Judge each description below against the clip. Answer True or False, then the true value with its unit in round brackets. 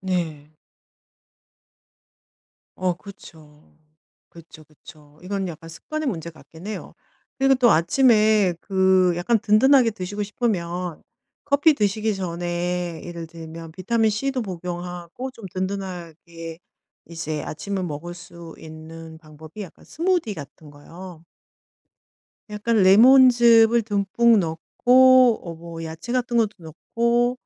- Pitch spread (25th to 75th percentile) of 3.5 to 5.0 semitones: False (5.4 semitones)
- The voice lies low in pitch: False (185 Hz)